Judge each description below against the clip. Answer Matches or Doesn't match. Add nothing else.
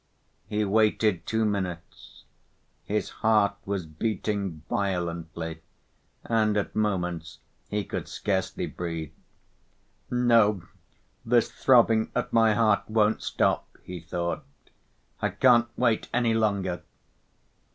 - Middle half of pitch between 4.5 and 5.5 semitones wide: Doesn't match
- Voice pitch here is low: Matches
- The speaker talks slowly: Matches